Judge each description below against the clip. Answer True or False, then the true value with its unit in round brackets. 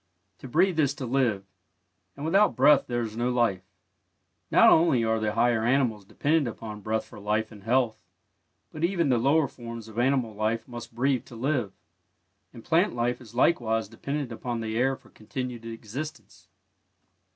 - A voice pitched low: True (120 Hz)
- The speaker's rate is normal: True (170 wpm)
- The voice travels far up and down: False (3.6 semitones)